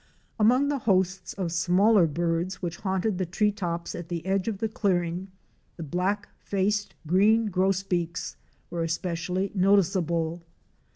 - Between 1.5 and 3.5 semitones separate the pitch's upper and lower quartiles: Yes, average, 2.8 semitones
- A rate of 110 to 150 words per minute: Yes, average, 140 wpm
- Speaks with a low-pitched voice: No, medium, 185 Hz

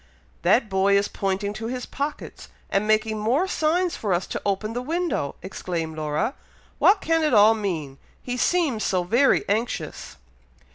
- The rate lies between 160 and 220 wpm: Yes, average, 170 wpm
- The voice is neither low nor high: No, high, 215 Hz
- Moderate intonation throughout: No, wide, 5.9 semitones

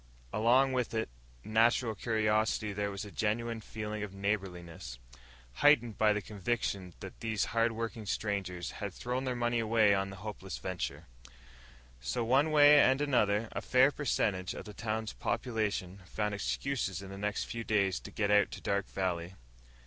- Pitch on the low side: Yes, low, 105 Hz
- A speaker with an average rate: Yes, average, 165 wpm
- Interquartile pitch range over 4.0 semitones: No, average, 3.0 semitones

